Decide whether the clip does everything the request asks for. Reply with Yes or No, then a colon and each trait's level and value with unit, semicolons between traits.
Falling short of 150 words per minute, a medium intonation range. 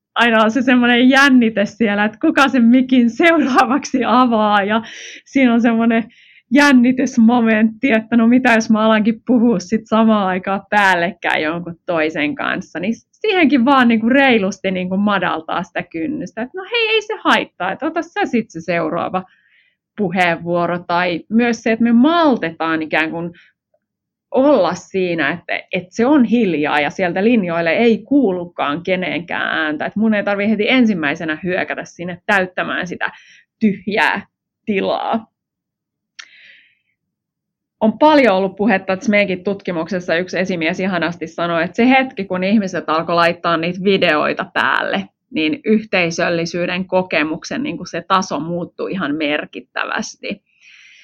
No: average, 140 wpm; wide, 5.8 semitones